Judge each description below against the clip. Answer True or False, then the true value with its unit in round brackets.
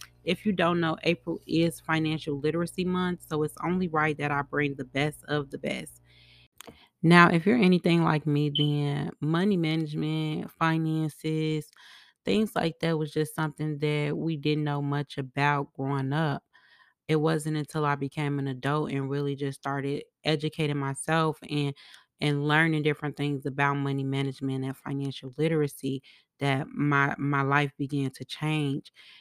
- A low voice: False (150 Hz)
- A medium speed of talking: True (155 wpm)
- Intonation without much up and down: True (2.1 semitones)